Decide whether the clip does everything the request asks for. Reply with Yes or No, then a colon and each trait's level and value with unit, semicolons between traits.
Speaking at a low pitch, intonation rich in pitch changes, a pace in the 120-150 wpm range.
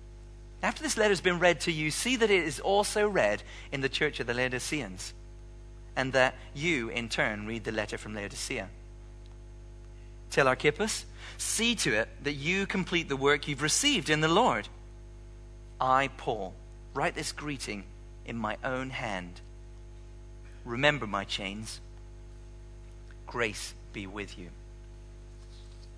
No: low, 115 Hz; average, 4.0 semitones; average, 140 wpm